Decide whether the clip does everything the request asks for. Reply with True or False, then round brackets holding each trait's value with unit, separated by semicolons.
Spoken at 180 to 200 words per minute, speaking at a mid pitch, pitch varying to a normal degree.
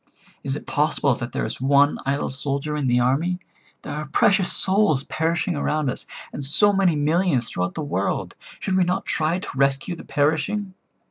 True (185 wpm; 150 Hz; 4.3 semitones)